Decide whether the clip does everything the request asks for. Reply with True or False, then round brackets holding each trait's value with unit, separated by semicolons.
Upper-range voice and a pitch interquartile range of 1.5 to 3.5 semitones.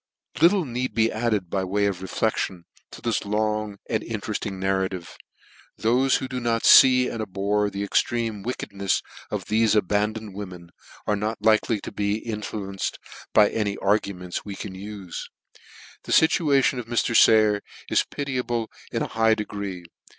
False (105 Hz; 2.4 semitones)